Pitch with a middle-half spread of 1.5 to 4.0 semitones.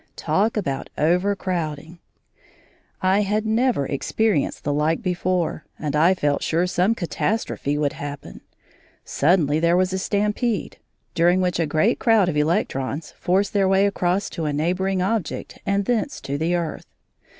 No: average, 4.5 semitones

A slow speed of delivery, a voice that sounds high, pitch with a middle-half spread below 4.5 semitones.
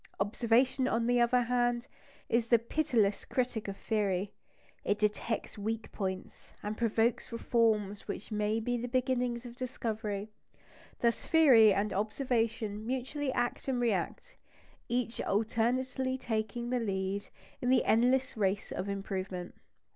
Yes: slow, 130 wpm; high, 230 Hz; average, 2.9 semitones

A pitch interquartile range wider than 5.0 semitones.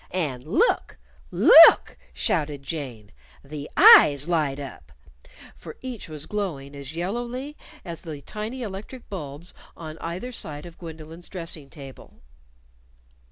Yes: wide, 5.4 semitones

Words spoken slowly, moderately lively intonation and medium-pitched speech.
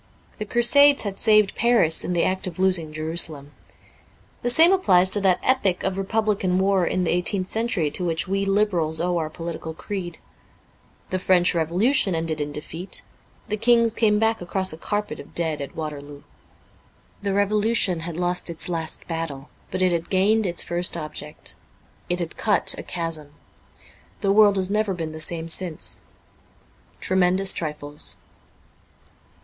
No: average, 165 wpm; average, 3.9 semitones; medium, 180 Hz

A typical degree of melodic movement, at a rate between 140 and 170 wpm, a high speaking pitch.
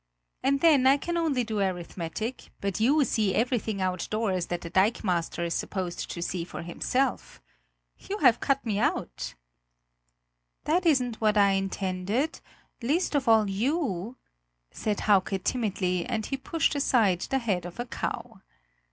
No: wide, 6.0 semitones; average, 150 wpm; high, 215 Hz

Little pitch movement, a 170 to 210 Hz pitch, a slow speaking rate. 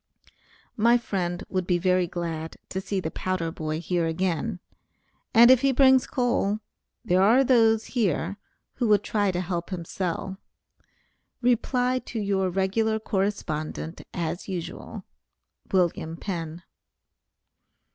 No: average, 4.3 semitones; high, 190 Hz; slow, 125 wpm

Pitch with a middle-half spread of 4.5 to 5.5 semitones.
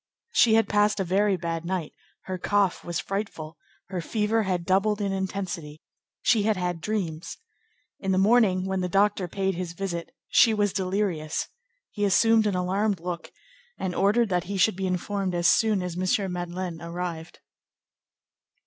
No: narrow, 2.6 semitones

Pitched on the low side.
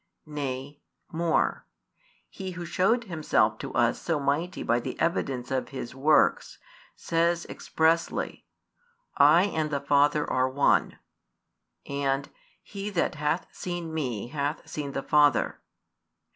No: medium, 150 Hz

